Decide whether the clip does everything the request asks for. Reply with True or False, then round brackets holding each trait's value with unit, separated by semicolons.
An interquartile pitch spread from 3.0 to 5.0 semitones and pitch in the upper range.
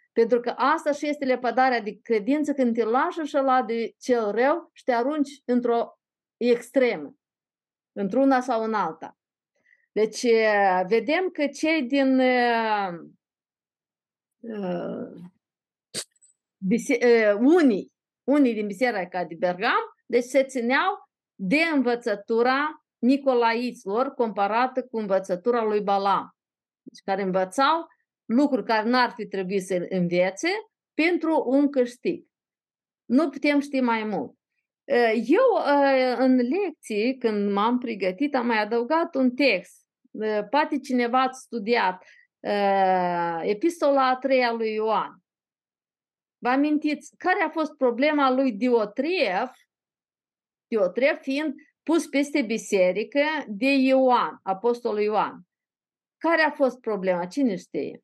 True (4.5 semitones; 250 Hz)